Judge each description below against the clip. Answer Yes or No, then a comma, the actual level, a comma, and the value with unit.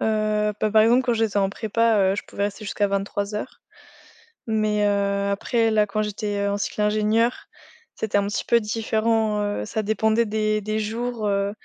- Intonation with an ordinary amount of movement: No, narrow, 1.4 semitones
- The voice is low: No, high, 215 Hz